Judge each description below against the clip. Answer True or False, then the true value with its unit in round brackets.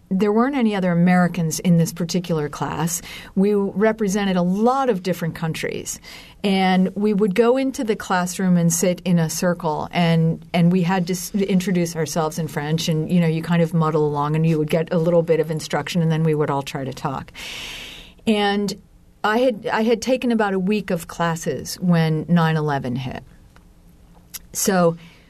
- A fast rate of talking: False (185 wpm)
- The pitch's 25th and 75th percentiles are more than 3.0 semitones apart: True (3.7 semitones)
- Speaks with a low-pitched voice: False (175 Hz)